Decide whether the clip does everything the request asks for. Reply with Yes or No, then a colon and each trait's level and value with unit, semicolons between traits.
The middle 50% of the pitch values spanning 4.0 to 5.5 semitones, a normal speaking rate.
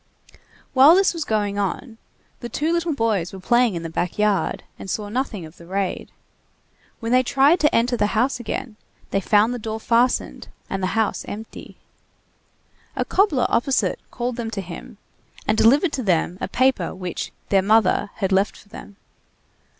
Yes: average, 4.4 semitones; average, 175 wpm